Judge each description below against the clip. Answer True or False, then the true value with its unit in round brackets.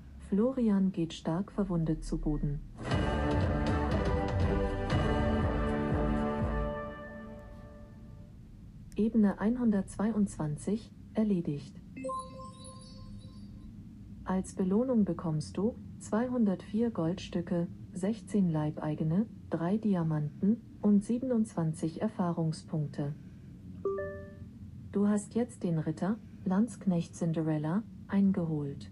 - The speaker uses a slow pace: True (60 wpm)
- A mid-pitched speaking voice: True (165 Hz)